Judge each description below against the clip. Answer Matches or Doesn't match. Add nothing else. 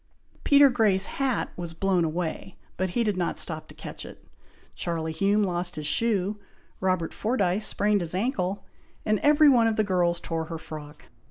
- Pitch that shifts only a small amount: Doesn't match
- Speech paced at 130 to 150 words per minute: Doesn't match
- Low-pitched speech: Doesn't match